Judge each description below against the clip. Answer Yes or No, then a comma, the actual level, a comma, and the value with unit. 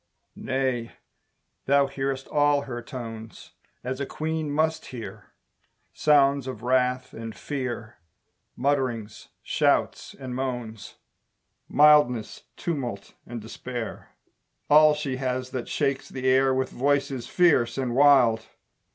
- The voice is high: No, low, 130 Hz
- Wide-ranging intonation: No, average, 2.7 semitones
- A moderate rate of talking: No, slow, 115 wpm